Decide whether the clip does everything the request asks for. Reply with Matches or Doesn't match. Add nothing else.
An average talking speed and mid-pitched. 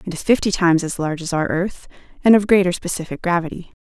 Doesn't match